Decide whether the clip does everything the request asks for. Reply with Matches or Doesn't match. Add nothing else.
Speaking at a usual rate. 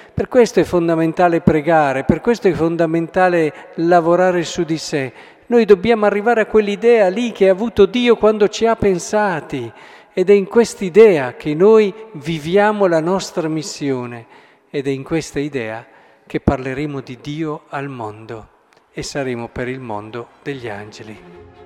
Matches